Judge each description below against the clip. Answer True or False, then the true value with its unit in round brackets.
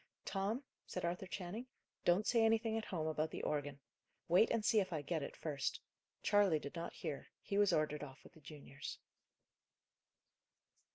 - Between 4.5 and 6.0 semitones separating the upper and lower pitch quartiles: True (5.4 semitones)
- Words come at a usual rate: True (170 wpm)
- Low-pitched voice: False (175 Hz)